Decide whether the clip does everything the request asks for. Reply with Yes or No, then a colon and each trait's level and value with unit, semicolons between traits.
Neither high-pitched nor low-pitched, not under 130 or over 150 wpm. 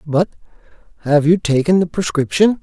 Yes: medium, 165 Hz; slow, 135 wpm